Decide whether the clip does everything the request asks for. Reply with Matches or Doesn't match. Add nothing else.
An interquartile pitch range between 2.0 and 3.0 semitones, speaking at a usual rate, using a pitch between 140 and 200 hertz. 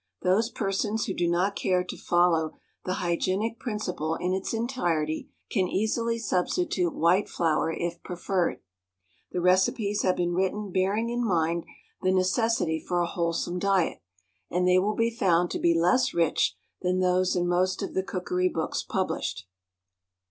Matches